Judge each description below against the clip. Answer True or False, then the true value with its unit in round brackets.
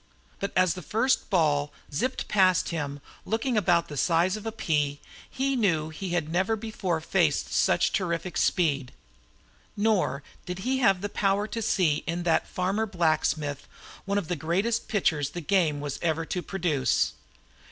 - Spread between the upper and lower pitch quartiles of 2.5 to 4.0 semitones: False (4.5 semitones)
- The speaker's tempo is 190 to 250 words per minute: False (160 wpm)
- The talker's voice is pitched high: False (180 Hz)